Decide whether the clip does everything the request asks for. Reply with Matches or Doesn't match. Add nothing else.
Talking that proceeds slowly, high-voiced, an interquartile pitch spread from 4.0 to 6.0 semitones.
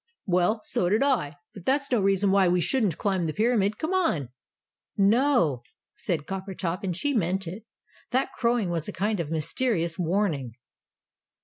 Doesn't match